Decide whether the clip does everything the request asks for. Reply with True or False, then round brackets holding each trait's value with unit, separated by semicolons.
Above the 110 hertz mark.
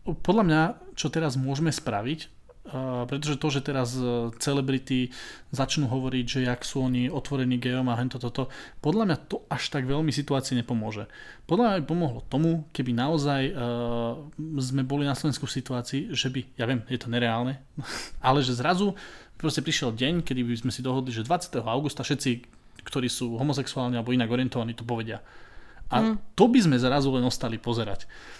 True (130 Hz)